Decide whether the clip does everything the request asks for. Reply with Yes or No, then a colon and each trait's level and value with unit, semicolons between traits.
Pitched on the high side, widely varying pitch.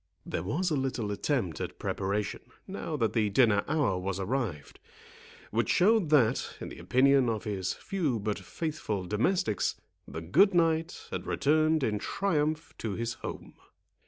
No: low, 120 Hz; wide, 7.3 semitones